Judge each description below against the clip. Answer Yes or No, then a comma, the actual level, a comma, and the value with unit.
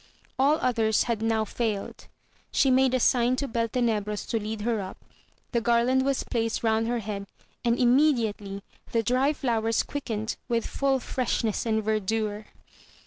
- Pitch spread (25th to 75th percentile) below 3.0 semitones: Yes, narrow, 2.5 semitones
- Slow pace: No, average, 150 wpm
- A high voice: Yes, high, 230 Hz